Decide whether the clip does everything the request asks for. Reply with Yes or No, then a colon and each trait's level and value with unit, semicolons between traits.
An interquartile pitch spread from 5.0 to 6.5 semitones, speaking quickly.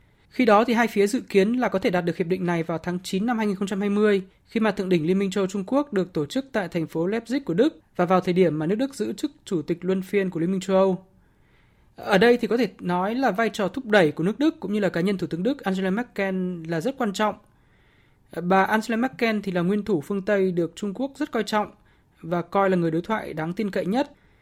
No: average, 3.7 semitones; fast, 270 wpm